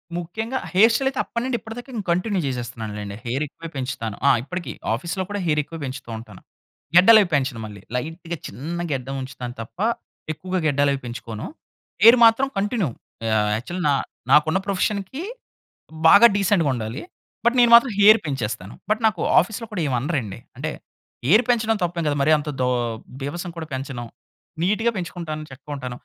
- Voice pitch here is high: No, medium, 165 Hz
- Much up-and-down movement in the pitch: Yes, wide, 7.9 semitones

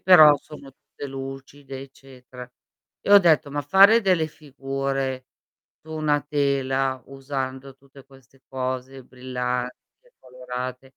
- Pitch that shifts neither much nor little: No, narrow, 2.0 semitones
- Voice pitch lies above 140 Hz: No, low, 135 Hz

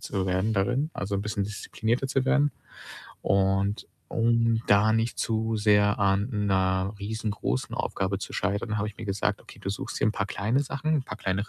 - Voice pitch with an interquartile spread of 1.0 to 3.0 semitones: Yes, narrow, 2.4 semitones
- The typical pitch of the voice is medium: No, low, 105 Hz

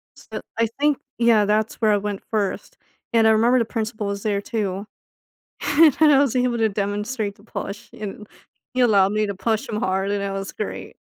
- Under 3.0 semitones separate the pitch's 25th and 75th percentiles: Yes, narrow, 2.5 semitones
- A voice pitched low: No, high, 215 Hz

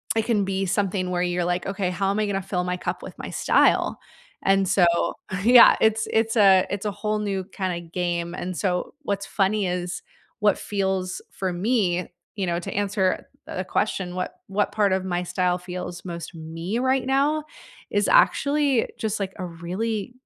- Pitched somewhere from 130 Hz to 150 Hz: No, high, 190 Hz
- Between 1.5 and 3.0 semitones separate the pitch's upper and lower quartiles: Yes, average, 2.7 semitones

